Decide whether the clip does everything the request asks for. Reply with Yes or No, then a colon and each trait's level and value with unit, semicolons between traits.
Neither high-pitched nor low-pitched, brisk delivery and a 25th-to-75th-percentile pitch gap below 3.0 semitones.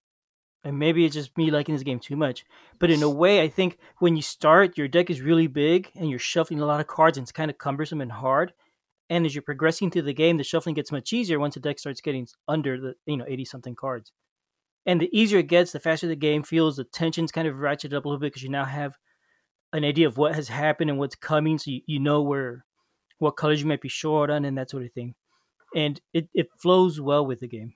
Yes: medium, 150 Hz; fast, 255 wpm; narrow, 2.5 semitones